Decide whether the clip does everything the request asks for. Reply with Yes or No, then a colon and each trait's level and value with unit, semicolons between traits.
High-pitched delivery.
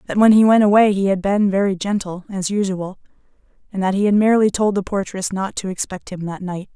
Yes: high, 195 Hz